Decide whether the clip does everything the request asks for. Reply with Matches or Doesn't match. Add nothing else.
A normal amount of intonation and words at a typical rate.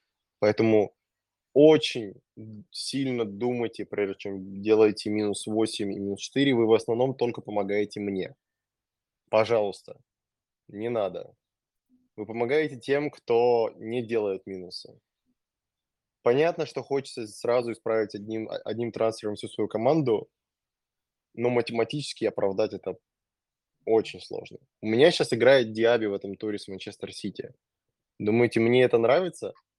Matches